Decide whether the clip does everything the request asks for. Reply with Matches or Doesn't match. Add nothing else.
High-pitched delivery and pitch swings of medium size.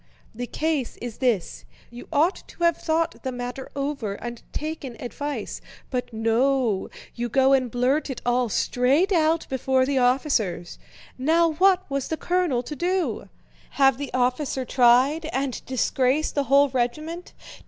Matches